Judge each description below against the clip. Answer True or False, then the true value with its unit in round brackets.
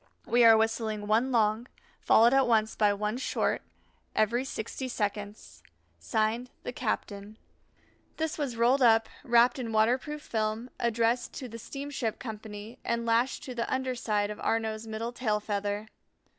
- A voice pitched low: False (230 Hz)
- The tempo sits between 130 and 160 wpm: True (150 wpm)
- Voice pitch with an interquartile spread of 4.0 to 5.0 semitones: False (2.4 semitones)